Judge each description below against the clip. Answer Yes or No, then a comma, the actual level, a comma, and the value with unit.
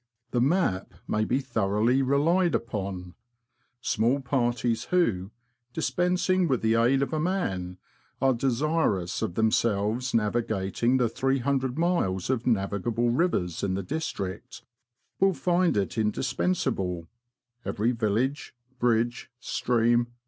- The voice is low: Yes, low, 120 Hz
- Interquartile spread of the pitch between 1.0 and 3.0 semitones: No, average, 4.8 semitones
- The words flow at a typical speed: No, slow, 120 wpm